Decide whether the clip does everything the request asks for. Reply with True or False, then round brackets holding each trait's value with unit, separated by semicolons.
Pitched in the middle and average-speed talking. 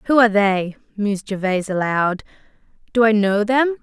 False (210 Hz; 155 wpm)